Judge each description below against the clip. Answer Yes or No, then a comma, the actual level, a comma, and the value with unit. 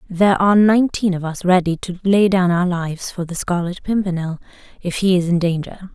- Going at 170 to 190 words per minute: No, average, 200 wpm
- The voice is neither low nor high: Yes, medium, 180 Hz